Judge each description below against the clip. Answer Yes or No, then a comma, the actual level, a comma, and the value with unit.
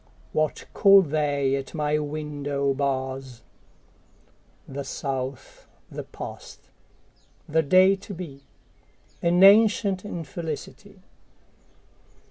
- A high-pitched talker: No, medium, 150 Hz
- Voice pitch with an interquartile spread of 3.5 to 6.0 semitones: Yes, average, 4.9 semitones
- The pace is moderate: No, slow, 80 wpm